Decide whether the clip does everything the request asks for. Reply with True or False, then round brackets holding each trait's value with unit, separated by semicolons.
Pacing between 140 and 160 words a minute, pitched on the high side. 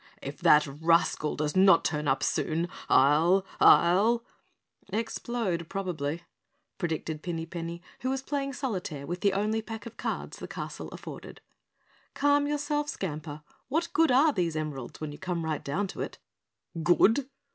False (155 wpm; 180 Hz)